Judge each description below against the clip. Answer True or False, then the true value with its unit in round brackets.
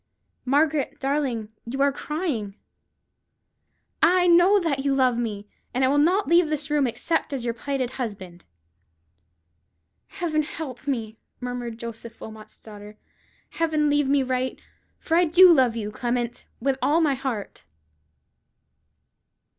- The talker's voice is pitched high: True (265 Hz)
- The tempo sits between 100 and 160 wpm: True (140 wpm)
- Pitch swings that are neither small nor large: True (4.7 semitones)